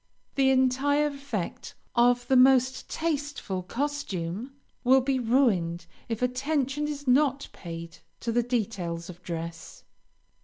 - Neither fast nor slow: No, slow, 120 wpm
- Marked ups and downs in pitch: Yes, wide, 6.5 semitones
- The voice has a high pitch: Yes, very high, 250 Hz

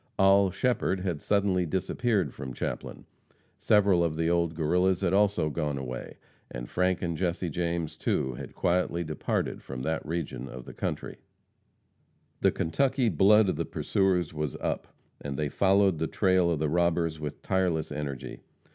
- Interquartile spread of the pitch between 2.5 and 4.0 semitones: Yes, average, 3.7 semitones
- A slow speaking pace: No, average, 155 wpm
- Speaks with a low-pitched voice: Yes, very low, 85 Hz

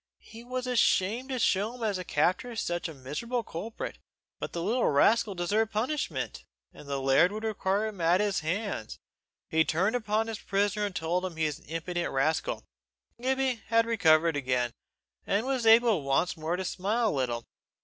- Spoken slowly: No, average, 185 wpm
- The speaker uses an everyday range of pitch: No, wide, 5.9 semitones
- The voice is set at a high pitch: Yes, high, 200 Hz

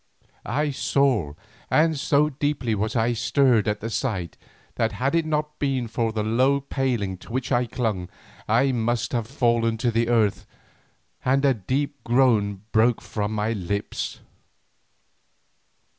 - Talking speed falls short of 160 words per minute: Yes, average, 145 wpm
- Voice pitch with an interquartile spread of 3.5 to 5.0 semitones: Yes, average, 3.9 semitones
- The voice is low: Yes, low, 120 Hz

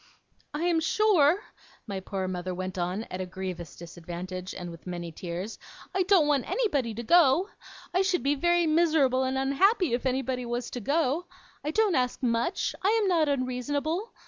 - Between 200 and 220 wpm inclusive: No, average, 175 wpm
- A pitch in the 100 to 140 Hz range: No, very high, 265 Hz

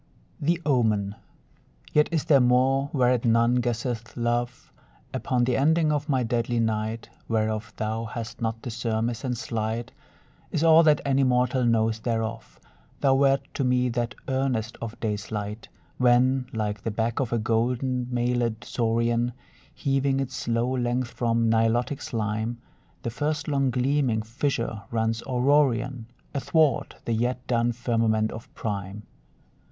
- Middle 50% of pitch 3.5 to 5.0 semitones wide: No, narrow, 2.6 semitones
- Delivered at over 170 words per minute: No, average, 145 wpm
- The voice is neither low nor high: No, low, 120 Hz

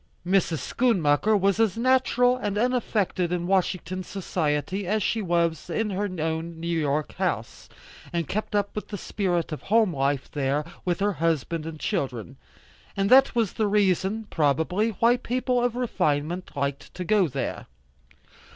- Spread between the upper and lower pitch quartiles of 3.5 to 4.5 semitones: No, average, 4.9 semitones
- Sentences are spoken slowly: No, average, 150 wpm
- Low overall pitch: No, medium, 185 Hz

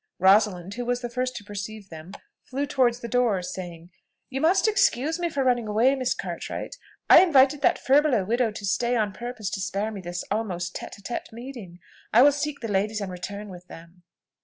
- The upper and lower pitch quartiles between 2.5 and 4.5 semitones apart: No, average, 4.9 semitones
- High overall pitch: Yes, high, 220 Hz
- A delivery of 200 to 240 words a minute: Yes, fast, 205 wpm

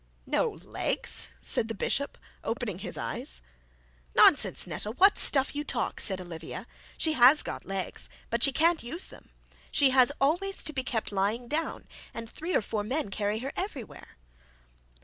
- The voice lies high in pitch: Yes, high, 245 Hz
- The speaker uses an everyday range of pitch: No, wide, 6.2 semitones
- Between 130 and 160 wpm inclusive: No, average, 170 wpm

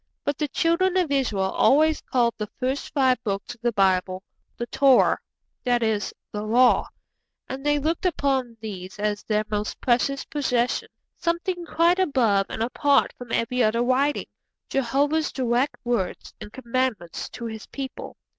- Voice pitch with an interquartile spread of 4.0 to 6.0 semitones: Yes, average, 4.5 semitones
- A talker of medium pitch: No, very high, 250 Hz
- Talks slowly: No, average, 155 wpm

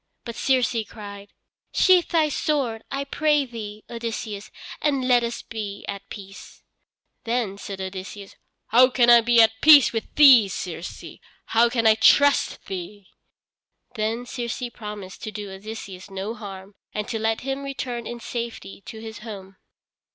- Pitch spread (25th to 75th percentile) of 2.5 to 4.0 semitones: Yes, average, 3.3 semitones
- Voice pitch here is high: Yes, high, 225 Hz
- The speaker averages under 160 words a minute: Yes, average, 150 wpm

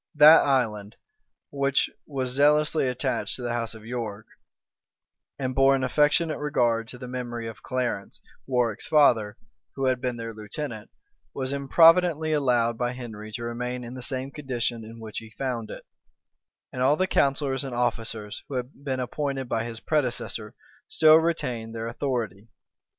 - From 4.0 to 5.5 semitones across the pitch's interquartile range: No, average, 3.2 semitones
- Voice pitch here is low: Yes, low, 125 Hz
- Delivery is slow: No, average, 160 wpm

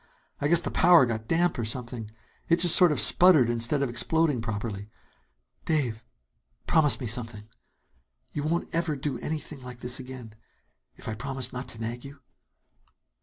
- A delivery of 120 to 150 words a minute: No, average, 165 wpm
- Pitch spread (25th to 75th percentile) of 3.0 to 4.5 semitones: No, average, 5.0 semitones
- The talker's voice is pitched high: No, low, 130 Hz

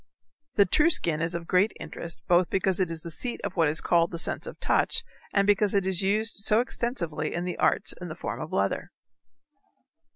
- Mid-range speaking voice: Yes, medium, 180 Hz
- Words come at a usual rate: No, fast, 215 wpm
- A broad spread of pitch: No, average, 3.3 semitones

